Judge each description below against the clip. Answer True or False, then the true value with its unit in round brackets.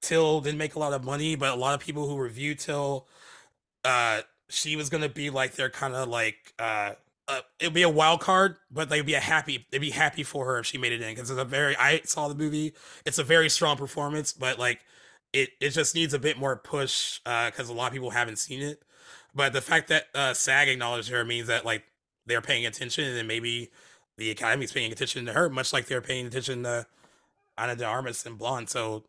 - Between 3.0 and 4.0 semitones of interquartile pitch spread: True (3.6 semitones)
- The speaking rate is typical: False (235 wpm)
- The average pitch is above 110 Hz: True (135 Hz)